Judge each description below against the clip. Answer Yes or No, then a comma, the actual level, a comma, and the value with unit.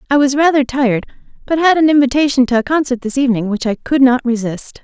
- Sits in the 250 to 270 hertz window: Yes, very high, 260 Hz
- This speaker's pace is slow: No, fast, 225 wpm